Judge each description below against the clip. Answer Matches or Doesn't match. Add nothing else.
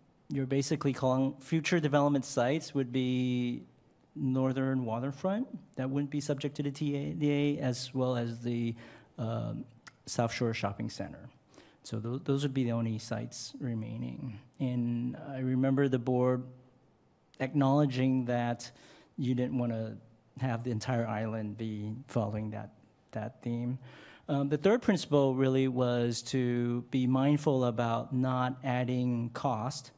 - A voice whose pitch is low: Matches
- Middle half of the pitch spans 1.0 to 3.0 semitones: Matches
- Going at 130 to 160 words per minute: Matches